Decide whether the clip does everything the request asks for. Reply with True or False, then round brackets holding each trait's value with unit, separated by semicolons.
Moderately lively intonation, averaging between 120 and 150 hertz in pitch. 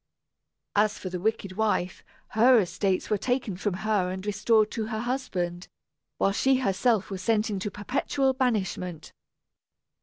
False (3.4 semitones; 210 Hz)